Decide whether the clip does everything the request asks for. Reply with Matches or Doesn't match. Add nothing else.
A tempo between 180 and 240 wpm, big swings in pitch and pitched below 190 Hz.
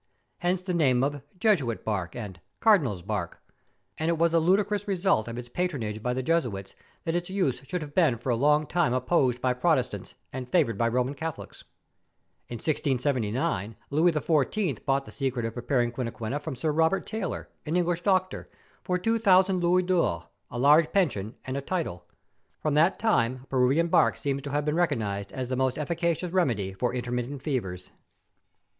Matches